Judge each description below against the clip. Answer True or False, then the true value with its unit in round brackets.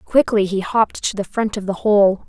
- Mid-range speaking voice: False (205 Hz)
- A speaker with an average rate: False (235 wpm)